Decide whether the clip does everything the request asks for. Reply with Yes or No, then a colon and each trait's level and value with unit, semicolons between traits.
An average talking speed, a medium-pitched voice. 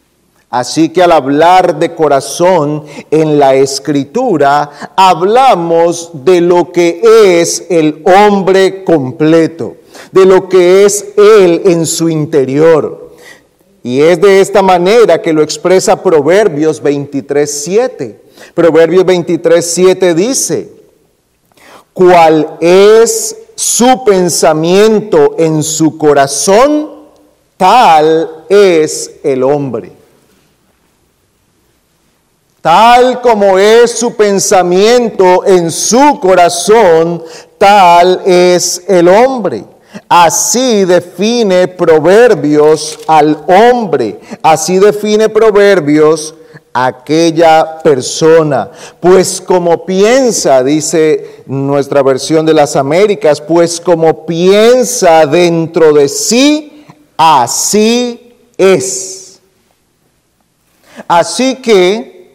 No: slow, 85 wpm; medium, 180 Hz